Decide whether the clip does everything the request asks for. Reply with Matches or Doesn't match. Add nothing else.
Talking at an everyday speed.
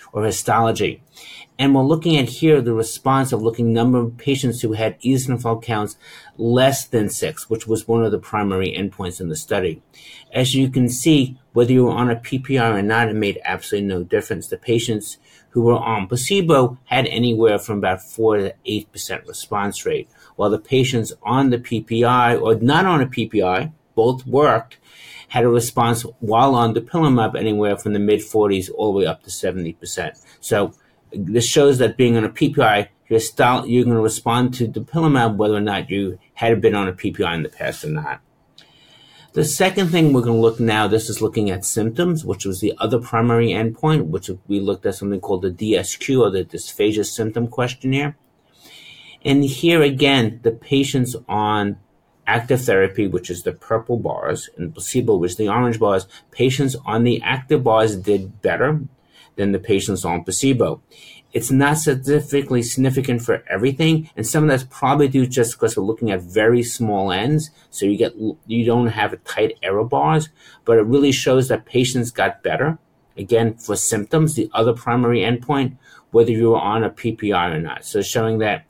Matches